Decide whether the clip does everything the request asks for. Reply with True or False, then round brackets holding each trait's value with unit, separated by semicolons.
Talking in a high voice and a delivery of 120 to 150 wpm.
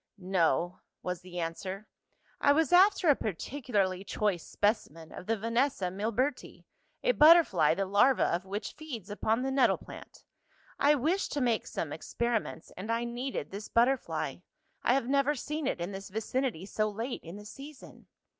False (225 Hz; 165 wpm)